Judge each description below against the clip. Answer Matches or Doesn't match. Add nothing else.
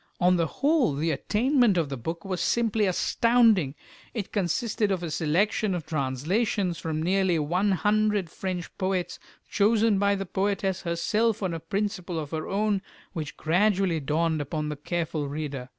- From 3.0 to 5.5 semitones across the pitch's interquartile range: Matches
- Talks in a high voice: Doesn't match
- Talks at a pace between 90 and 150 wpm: Doesn't match